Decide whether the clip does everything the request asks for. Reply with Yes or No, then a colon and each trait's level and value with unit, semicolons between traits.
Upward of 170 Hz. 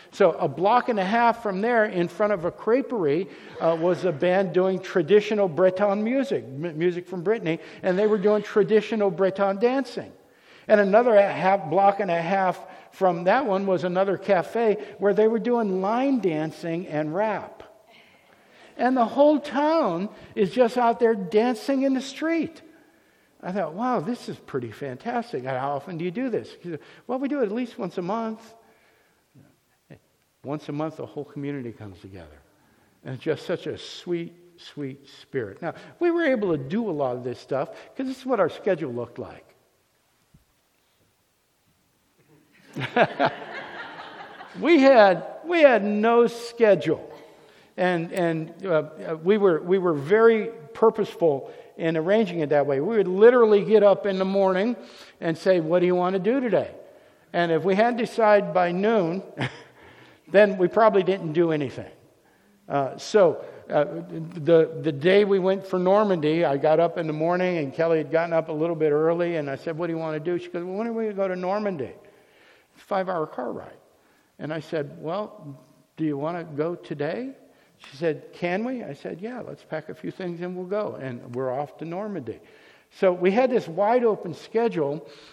Yes: high, 190 Hz